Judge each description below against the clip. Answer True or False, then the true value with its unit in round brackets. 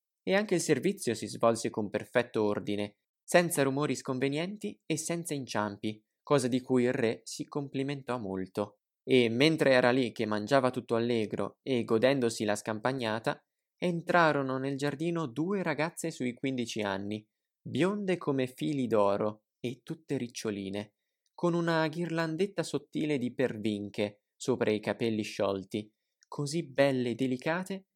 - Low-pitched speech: True (130 Hz)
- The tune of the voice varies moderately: False (6.2 semitones)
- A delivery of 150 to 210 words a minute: False (135 wpm)